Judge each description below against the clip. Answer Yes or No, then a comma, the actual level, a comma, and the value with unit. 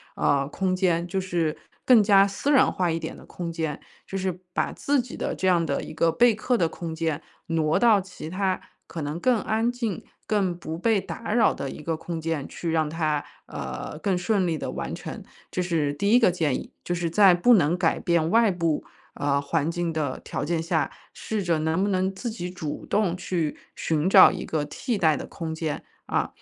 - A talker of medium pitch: Yes, medium, 175 Hz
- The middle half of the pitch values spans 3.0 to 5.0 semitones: Yes, average, 3.5 semitones